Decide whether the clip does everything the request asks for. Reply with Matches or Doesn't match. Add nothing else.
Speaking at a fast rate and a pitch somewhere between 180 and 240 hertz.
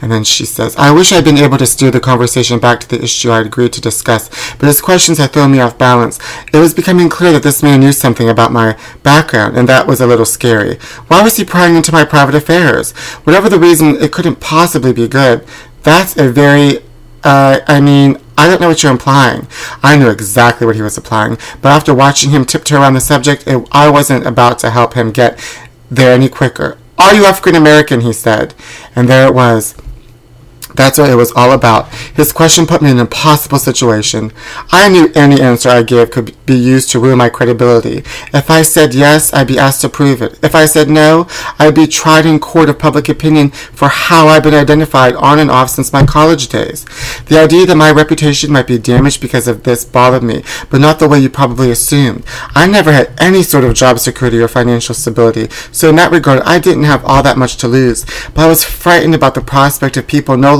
Doesn't match